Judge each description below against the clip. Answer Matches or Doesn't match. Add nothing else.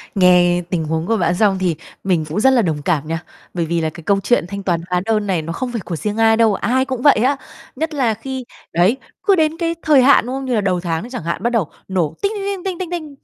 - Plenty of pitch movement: Matches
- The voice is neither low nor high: Doesn't match